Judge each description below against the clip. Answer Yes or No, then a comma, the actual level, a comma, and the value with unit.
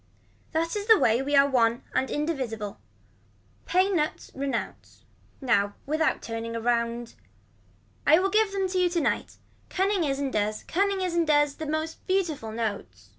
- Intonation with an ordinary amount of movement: No, wide, 7.3 semitones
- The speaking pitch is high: Yes, very high, 290 Hz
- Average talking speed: Yes, average, 160 wpm